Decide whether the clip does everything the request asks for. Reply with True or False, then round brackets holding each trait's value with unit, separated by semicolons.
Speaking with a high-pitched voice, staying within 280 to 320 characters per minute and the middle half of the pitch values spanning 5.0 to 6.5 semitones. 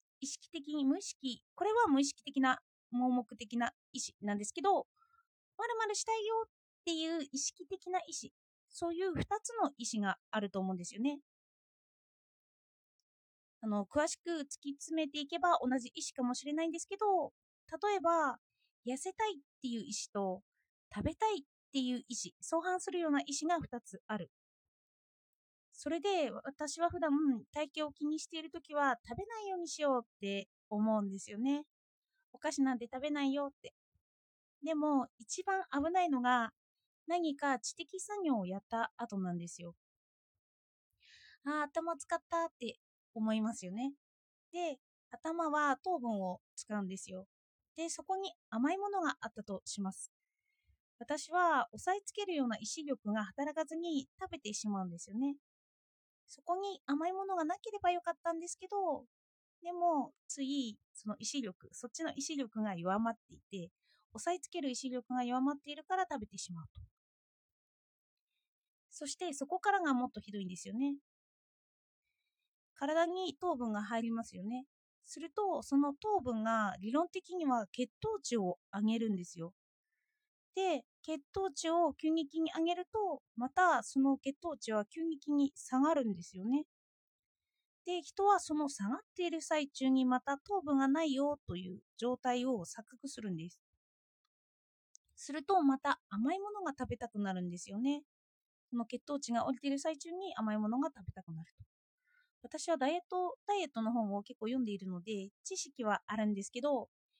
False (280 Hz; 305 characters per minute; 6.9 semitones)